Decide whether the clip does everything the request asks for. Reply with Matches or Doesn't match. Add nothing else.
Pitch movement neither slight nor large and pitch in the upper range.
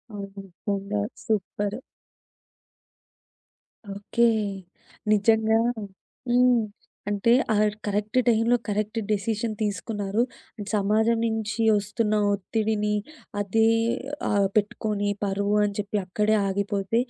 Doesn't match